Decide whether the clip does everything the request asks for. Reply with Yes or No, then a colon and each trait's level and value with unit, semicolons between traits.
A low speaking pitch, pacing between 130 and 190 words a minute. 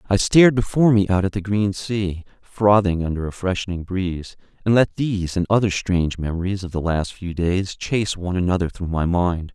No: very low, 95 Hz; average, 200 wpm